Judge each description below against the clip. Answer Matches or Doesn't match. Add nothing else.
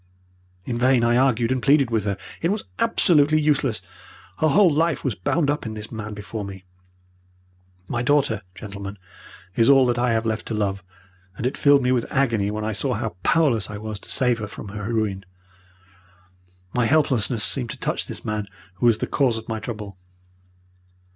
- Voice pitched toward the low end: Matches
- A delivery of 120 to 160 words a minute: Doesn't match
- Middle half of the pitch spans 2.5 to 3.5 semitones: Doesn't match